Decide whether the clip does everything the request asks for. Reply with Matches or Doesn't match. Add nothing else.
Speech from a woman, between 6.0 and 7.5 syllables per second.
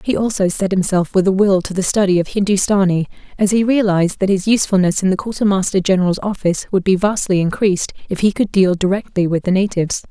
Matches